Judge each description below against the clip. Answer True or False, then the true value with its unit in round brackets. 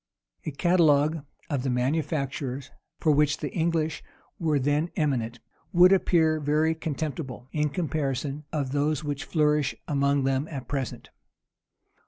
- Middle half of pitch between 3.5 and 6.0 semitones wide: False (2.4 semitones)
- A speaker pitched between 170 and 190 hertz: False (150 Hz)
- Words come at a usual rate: False (130 wpm)